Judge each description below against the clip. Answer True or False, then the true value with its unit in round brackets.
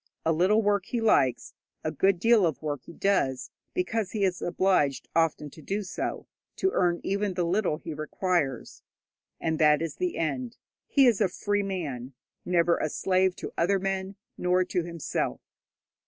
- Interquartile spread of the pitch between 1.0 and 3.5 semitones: False (3.9 semitones)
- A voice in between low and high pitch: True (180 Hz)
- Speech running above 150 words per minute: True (170 wpm)